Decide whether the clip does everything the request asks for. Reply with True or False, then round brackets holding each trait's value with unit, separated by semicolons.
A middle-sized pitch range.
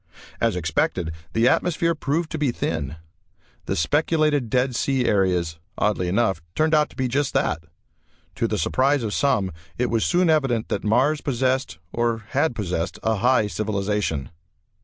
False (6.2 semitones)